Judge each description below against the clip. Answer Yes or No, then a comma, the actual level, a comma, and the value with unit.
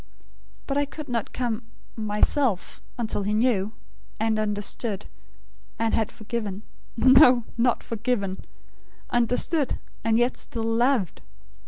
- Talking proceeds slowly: Yes, slow, 115 wpm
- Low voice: No, high, 230 Hz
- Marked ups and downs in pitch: No, average, 2.8 semitones